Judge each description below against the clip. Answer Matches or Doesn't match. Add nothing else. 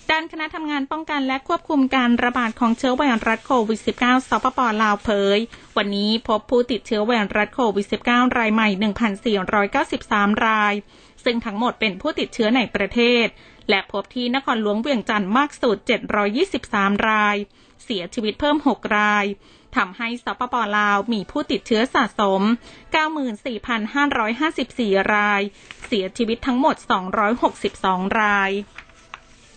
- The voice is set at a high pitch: Matches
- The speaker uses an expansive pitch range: Doesn't match